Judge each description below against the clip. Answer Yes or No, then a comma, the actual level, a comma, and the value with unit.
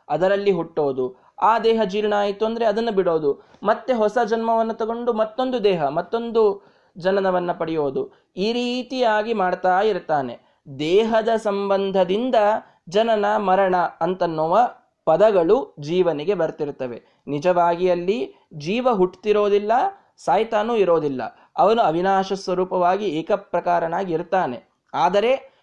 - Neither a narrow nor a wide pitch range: Yes, average, 4.3 semitones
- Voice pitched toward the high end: Yes, high, 195 Hz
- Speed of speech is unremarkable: Yes, average, 95 wpm